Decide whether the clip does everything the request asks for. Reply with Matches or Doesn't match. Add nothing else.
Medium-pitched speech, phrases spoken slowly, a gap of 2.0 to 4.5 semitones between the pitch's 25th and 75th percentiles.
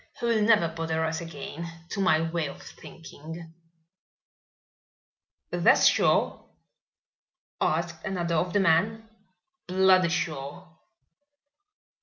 Matches